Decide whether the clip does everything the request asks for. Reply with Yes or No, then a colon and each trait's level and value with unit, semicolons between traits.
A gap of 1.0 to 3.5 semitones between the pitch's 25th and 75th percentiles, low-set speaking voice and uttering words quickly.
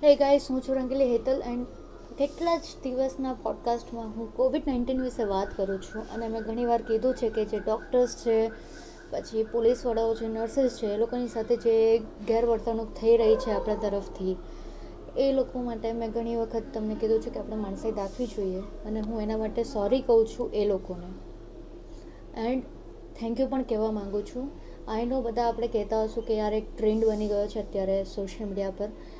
No: narrow, 2.5 semitones; high, 230 Hz; fast, 180 wpm